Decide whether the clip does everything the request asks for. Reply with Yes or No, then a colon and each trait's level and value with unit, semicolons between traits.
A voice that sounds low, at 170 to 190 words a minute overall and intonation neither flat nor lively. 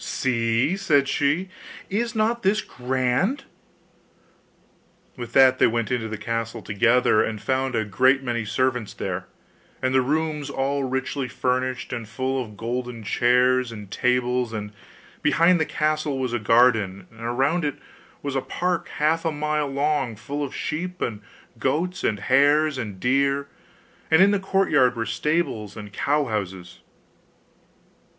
No: low, 130 Hz; average, 150 wpm; average, 4.4 semitones